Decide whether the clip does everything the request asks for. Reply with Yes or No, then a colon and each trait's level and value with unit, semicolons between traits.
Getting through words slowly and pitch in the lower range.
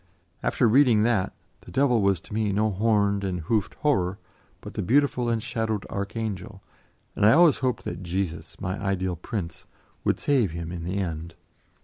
No: average, 165 wpm; low, 100 Hz